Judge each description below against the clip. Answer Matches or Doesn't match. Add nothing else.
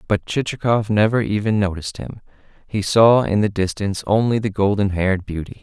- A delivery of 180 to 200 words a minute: Doesn't match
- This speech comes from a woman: Doesn't match